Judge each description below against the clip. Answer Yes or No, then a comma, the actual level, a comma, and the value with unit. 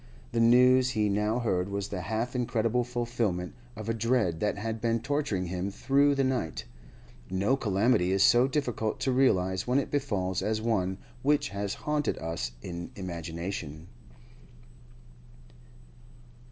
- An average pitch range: Yes, average, 4.9 semitones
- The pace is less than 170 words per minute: Yes, average, 140 wpm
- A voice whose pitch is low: Yes, low, 110 Hz